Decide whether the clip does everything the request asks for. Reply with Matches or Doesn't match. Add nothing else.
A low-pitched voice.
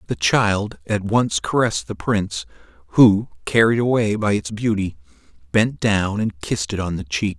Matches